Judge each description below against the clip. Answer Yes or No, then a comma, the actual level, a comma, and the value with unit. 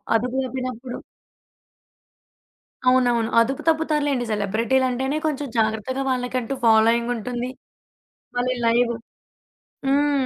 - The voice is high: Yes, very high, 250 Hz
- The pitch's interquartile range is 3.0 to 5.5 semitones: No, narrow, 2.4 semitones